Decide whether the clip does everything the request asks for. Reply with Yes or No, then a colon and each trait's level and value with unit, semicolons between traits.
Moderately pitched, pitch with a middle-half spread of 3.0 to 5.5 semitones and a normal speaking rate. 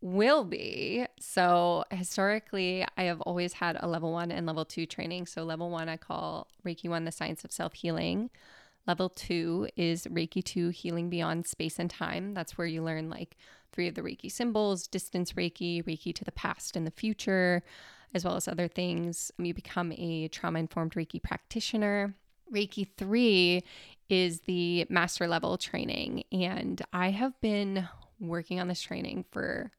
No: medium, 175 Hz; narrow, 2.5 semitones; average, 170 wpm